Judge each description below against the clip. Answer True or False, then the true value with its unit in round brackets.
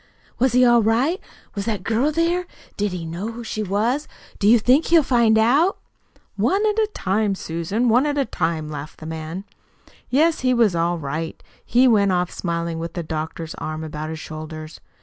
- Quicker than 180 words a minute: True (190 wpm)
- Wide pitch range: True (7.3 semitones)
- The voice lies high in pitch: True (210 Hz)